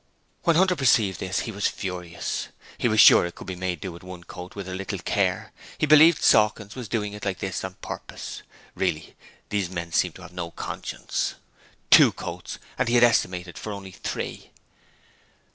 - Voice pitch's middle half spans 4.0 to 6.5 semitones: No, average, 3.4 semitones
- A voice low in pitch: Yes, very low, 95 Hz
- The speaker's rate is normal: Yes, average, 195 wpm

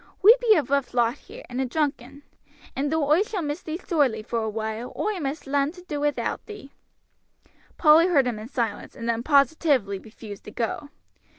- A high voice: Yes, very high, 280 Hz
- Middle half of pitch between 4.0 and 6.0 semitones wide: Yes, average, 5.1 semitones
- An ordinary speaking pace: Yes, average, 190 wpm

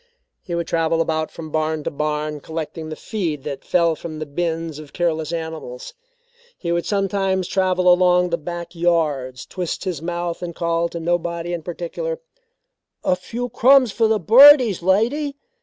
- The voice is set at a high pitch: No, medium, 170 Hz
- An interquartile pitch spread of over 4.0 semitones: No, average, 2.9 semitones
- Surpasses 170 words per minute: No, average, 165 wpm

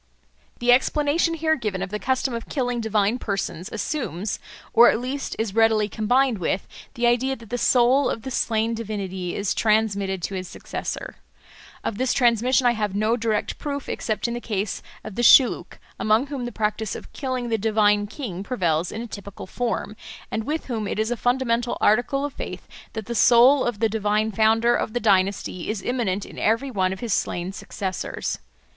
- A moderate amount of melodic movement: Yes, average, 3.1 semitones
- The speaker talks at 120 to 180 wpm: No, average, 190 wpm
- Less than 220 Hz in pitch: No, high, 225 Hz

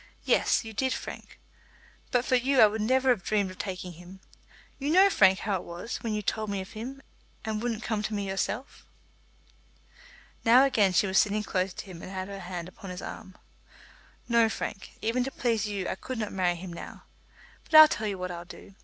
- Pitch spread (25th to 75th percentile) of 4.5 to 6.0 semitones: No, average, 3.9 semitones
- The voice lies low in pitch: No, high, 210 Hz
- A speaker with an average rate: No, fast, 215 wpm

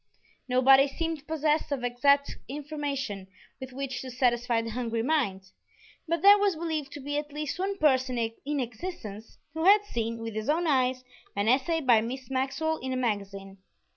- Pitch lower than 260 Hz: No, very high, 265 Hz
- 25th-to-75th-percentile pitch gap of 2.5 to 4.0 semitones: No, average, 4.4 semitones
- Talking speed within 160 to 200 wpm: Yes, average, 170 wpm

